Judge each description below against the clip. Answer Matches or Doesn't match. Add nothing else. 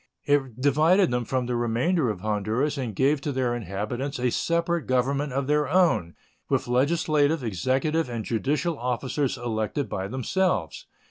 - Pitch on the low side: Matches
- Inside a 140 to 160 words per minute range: Matches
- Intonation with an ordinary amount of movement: Matches